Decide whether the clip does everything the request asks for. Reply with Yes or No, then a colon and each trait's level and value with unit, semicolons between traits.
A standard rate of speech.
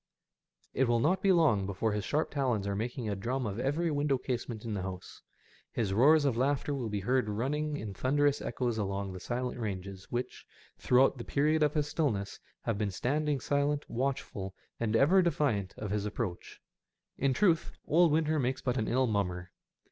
Yes: average, 185 wpm